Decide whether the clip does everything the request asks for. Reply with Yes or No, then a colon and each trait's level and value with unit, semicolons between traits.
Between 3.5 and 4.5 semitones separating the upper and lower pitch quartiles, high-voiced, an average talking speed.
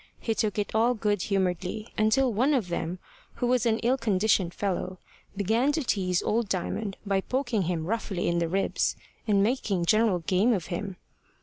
Yes: average, 3.8 semitones; high, 205 Hz; average, 180 wpm